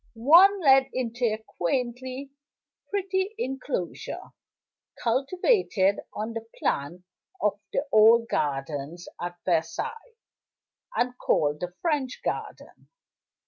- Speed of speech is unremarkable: No, slow, 100 wpm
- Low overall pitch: No, high, 235 Hz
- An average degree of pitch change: No, wide, 7.8 semitones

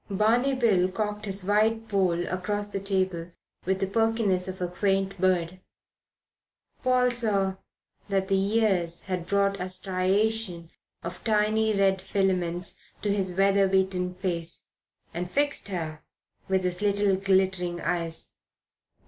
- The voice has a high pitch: Yes, high, 195 Hz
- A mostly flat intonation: Yes, narrow, 2.2 semitones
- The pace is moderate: No, slow, 130 wpm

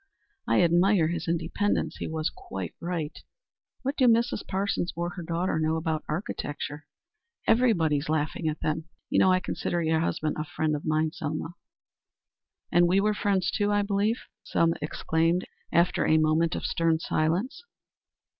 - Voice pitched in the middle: Yes, medium, 165 Hz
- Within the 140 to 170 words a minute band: Yes, average, 160 wpm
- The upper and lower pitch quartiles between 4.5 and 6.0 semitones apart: No, average, 3.3 semitones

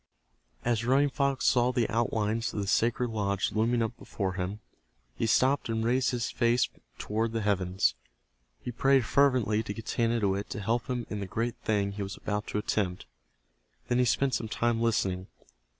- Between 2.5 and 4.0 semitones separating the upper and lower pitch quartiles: Yes, average, 2.8 semitones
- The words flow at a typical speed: Yes, average, 175 wpm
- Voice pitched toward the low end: Yes, low, 115 Hz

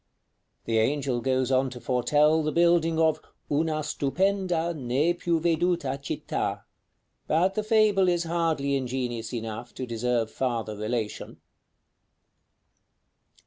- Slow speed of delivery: Yes, slow, 120 wpm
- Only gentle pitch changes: No, wide, 5.5 semitones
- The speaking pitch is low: No, medium, 145 Hz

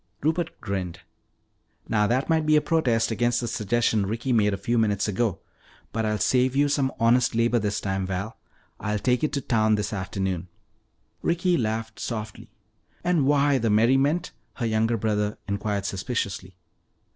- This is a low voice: Yes, low, 115 Hz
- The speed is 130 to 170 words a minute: Yes, average, 160 wpm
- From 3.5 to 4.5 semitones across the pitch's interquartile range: Yes, average, 3.8 semitones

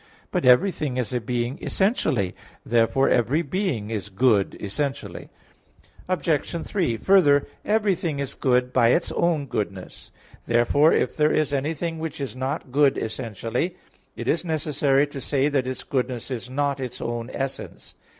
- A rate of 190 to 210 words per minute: No, average, 150 wpm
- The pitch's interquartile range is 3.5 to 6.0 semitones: Yes, average, 4.3 semitones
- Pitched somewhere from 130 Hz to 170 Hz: Yes, low, 135 Hz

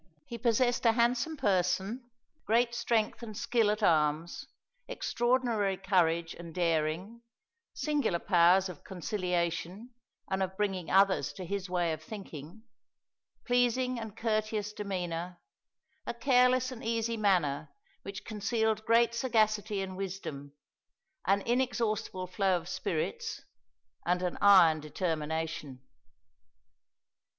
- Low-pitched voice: No, high, 200 Hz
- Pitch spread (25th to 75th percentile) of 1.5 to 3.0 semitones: No, average, 4.8 semitones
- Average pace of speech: No, slow, 115 wpm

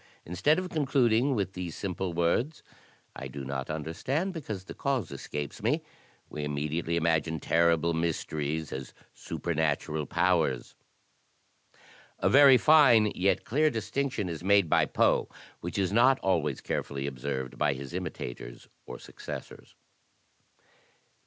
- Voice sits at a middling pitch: No, very low, 85 Hz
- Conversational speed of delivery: No, slow, 130 wpm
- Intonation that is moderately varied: No, wide, 7.6 semitones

